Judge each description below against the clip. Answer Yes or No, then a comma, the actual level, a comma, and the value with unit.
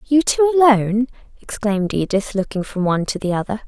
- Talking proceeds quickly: No, average, 180 wpm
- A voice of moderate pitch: No, high, 220 Hz